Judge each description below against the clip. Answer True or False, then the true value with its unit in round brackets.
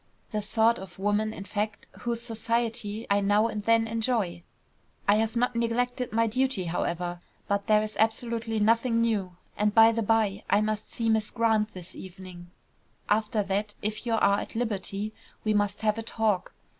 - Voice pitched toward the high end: True (215 Hz)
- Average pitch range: False (2.0 semitones)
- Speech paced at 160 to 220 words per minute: True (175 wpm)